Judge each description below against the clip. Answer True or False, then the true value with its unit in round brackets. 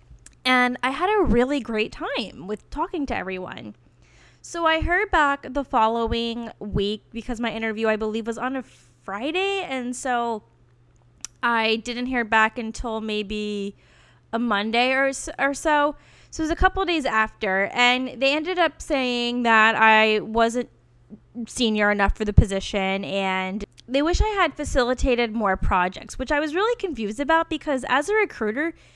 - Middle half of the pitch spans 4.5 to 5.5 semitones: True (5.0 semitones)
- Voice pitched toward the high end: True (240 Hz)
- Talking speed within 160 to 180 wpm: True (165 wpm)